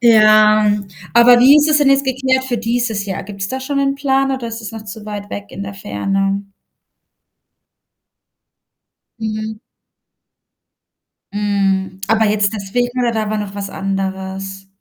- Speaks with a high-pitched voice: Yes, high, 215 Hz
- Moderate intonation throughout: Yes, average, 3.6 semitones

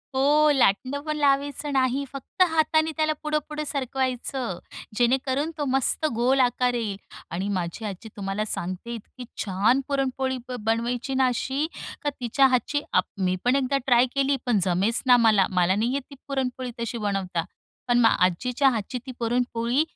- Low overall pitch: No, very high, 250 Hz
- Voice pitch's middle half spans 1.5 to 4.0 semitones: Yes, average, 3.6 semitones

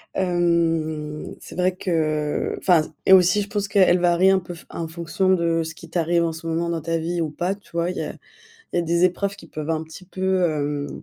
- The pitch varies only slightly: Yes, narrow, 2.2 semitones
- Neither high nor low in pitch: Yes, medium, 170 Hz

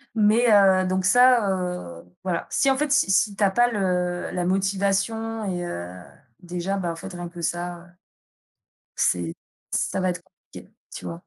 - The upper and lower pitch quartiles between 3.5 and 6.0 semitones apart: No, average, 2.8 semitones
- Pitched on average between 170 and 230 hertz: Yes, medium, 185 Hz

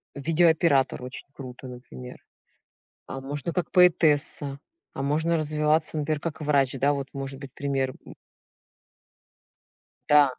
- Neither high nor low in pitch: Yes, medium, 145 Hz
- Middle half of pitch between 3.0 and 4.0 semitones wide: No, narrow, 2.4 semitones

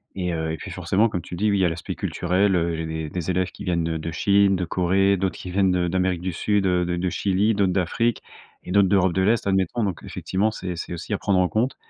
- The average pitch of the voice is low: Yes, very low, 95 Hz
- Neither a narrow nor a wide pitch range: No, narrow, 2.2 semitones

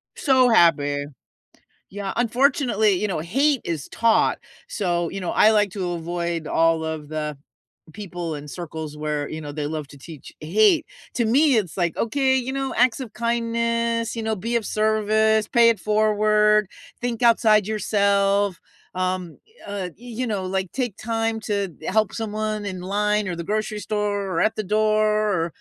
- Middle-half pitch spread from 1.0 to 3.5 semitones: No, average, 4.3 semitones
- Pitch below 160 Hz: No, high, 210 Hz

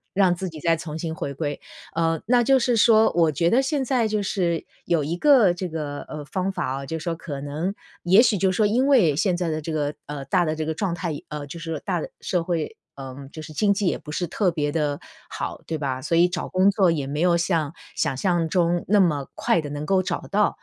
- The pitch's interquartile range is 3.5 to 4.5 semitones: Yes, average, 4.0 semitones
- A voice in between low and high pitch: Yes, medium, 170 Hz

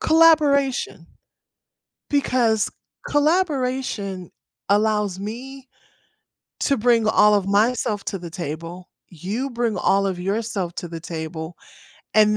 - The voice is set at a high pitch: Yes, high, 210 Hz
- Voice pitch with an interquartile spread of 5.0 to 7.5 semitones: Yes, wide, 5.6 semitones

